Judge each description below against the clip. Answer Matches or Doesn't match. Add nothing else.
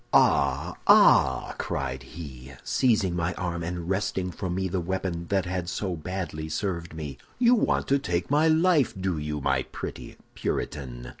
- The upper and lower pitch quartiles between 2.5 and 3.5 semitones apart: Doesn't match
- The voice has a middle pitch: Doesn't match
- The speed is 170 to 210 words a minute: Doesn't match